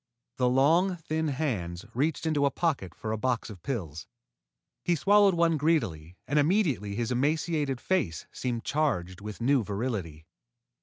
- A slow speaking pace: No, average, 150 wpm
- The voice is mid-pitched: No, low, 130 Hz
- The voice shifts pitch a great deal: Yes, wide, 7.5 semitones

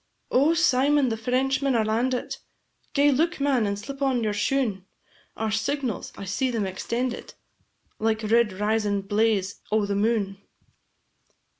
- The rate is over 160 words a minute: No, average, 140 wpm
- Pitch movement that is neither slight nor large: Yes, average, 4.3 semitones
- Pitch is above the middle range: Yes, high, 225 Hz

